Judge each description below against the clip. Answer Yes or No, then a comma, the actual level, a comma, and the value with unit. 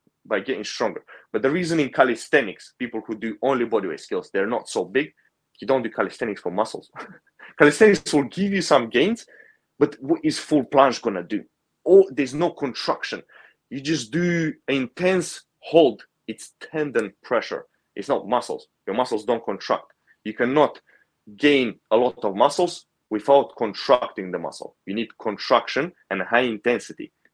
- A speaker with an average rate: Yes, average, 160 wpm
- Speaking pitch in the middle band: Yes, medium, 145 Hz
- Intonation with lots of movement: Yes, wide, 6.6 semitones